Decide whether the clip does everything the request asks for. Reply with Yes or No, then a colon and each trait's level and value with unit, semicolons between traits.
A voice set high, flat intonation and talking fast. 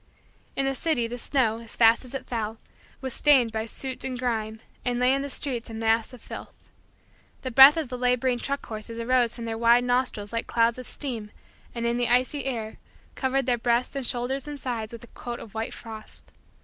Yes: high, 245 Hz; narrow, 2.2 semitones; fast, 215 wpm